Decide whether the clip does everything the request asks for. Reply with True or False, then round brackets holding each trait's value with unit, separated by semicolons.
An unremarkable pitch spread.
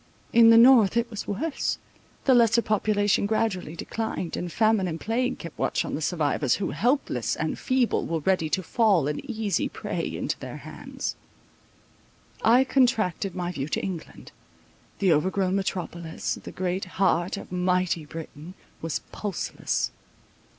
True (4.6 semitones)